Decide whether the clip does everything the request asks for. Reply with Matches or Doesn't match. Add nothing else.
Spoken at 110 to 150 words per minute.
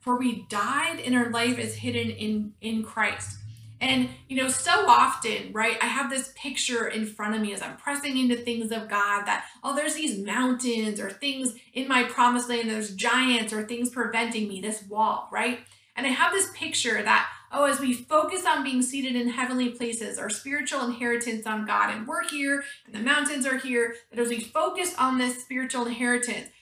Doesn't match